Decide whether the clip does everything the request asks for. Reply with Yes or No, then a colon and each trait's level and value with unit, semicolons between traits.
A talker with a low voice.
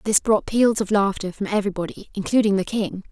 No: high, 205 Hz